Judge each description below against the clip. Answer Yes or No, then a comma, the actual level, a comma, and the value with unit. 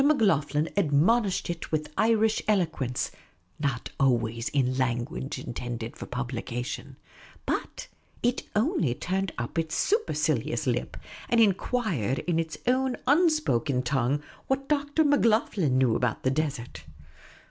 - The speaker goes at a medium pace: No, slow, 120 wpm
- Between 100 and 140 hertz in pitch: No, medium, 155 Hz